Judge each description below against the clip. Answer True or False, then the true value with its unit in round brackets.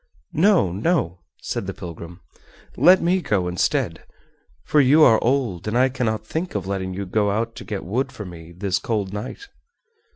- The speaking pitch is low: True (105 Hz)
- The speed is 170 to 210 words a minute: True (175 wpm)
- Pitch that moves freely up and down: True (6.4 semitones)